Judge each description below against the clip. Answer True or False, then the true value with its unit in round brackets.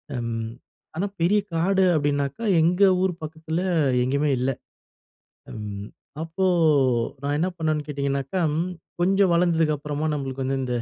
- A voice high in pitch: False (150 Hz)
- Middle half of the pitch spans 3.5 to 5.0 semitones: True (3.8 semitones)